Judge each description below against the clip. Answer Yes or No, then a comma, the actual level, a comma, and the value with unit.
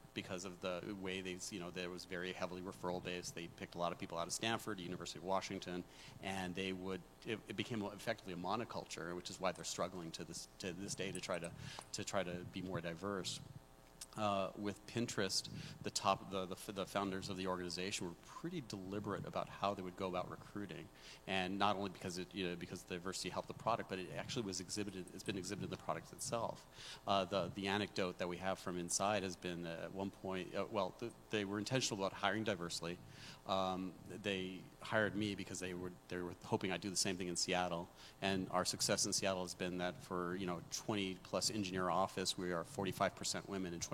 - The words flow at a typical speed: No, fast, 220 wpm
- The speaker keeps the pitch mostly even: Yes, narrow, 2.1 semitones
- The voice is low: Yes, very low, 95 Hz